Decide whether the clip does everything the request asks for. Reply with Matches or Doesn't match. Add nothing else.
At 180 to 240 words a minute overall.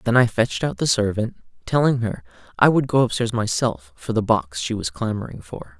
Matches